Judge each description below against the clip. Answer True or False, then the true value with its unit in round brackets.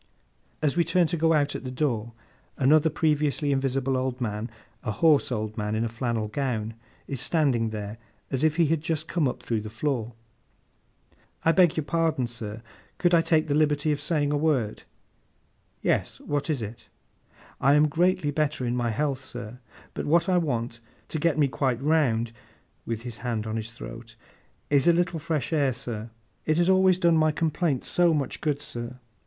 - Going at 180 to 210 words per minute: True (190 wpm)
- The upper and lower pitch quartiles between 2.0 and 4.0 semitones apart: False (5.0 semitones)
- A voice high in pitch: False (140 Hz)